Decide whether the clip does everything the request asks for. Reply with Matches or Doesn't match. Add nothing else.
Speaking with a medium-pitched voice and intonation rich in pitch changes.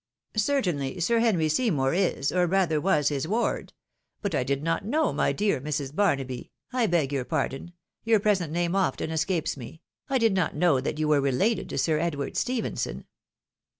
Matches